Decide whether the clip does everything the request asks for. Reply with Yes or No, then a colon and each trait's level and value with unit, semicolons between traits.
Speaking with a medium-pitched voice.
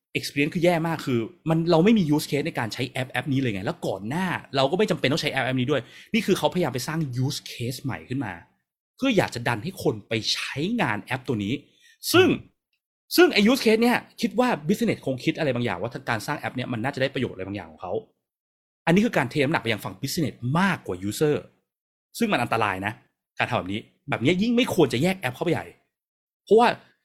Yes: medium, 145 Hz